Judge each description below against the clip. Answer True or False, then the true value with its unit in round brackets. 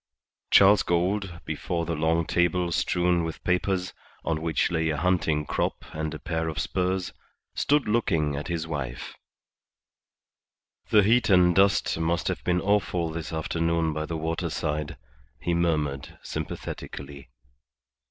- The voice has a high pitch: False (85 Hz)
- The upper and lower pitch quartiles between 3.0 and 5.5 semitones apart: False (2.4 semitones)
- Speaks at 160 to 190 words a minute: False (135 wpm)